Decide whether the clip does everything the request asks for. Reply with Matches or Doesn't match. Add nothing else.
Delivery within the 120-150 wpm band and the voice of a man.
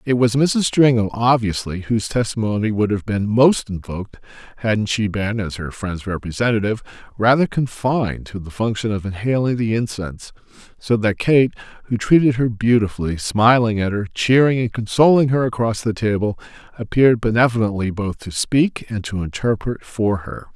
Doesn't match